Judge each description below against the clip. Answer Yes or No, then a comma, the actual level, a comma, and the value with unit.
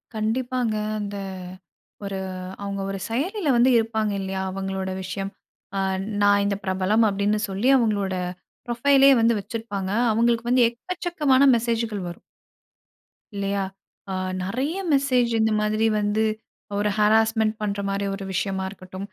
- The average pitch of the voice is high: Yes, high, 215 Hz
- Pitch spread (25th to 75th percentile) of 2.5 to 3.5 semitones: Yes, average, 3.2 semitones